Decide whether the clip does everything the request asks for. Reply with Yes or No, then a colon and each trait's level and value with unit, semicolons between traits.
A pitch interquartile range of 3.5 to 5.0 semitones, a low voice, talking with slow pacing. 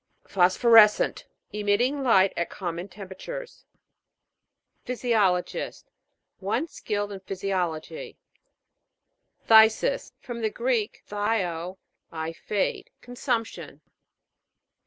No: average, 4.2 semitones; high, 210 Hz; slow, 80 wpm